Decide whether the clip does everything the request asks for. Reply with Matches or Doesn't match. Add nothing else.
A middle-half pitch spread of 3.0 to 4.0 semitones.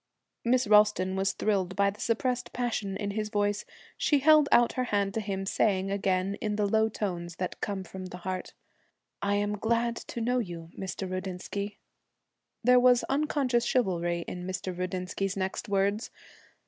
Matches